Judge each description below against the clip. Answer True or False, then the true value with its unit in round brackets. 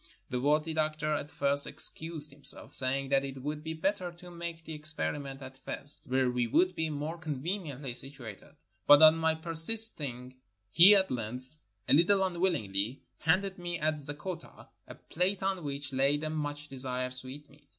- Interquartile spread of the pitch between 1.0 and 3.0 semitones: False (3.5 semitones)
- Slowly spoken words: False (170 wpm)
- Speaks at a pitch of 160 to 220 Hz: False (150 Hz)